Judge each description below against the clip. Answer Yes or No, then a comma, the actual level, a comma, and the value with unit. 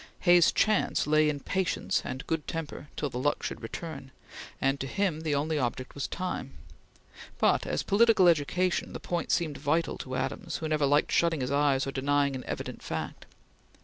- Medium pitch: Yes, medium, 150 Hz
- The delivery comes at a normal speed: Yes, average, 180 wpm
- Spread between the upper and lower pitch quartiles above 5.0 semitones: No, average, 3.4 semitones